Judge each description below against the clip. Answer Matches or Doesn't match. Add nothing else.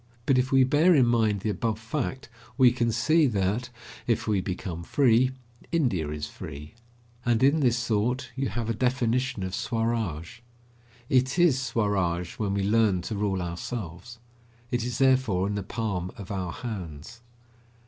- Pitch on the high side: Doesn't match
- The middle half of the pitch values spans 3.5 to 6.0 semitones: Matches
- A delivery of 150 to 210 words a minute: Matches